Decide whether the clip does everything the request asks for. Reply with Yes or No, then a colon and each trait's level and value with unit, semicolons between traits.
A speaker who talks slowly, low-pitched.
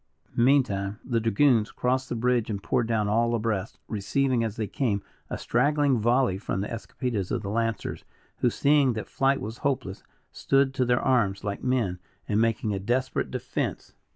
No: average, 175 wpm; low, 115 Hz